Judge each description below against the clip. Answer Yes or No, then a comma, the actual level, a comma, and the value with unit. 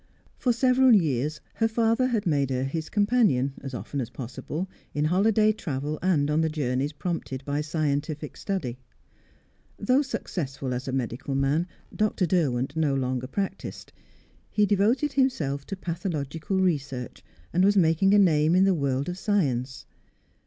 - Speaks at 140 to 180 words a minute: Yes, average, 150 wpm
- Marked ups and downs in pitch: Yes, wide, 6.3 semitones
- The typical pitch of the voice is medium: Yes, medium, 155 Hz